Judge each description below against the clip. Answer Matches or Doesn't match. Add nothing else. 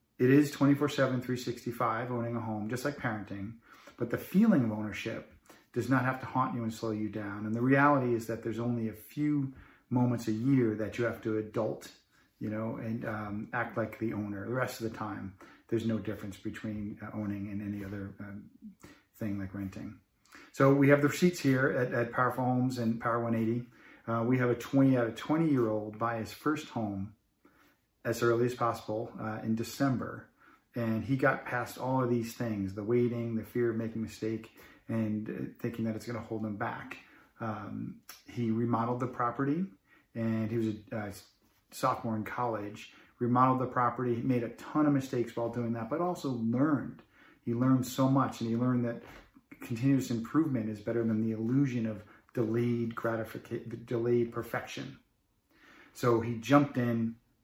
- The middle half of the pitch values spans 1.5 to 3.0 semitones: Matches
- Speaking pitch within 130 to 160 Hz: Doesn't match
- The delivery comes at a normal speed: Matches